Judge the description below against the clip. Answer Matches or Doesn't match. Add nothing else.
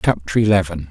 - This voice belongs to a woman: Doesn't match